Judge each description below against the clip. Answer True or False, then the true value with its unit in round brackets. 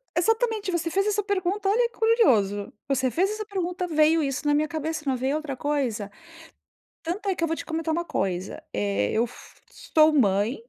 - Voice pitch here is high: True (320 Hz)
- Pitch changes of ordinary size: False (7.0 semitones)